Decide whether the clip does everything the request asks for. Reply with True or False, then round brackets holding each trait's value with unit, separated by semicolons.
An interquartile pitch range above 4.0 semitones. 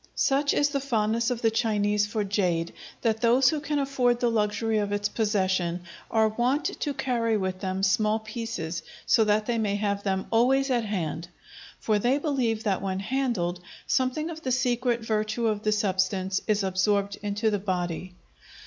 False (3.4 semitones)